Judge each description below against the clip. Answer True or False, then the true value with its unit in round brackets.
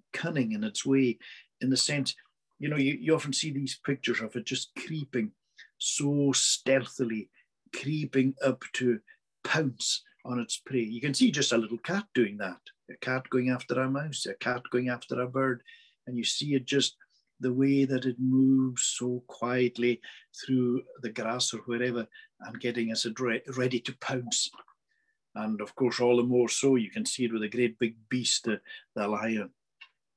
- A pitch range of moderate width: False (2.3 semitones)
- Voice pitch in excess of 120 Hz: True (130 Hz)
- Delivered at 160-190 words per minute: True (180 wpm)